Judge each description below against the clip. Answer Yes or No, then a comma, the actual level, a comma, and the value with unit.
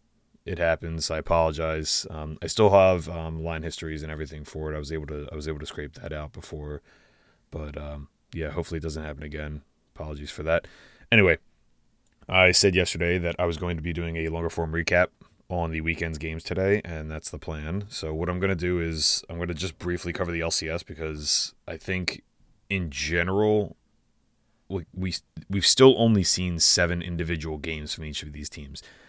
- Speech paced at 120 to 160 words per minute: No, average, 195 wpm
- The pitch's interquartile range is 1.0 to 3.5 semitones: Yes, narrow, 2.5 semitones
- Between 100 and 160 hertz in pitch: No, very low, 85 Hz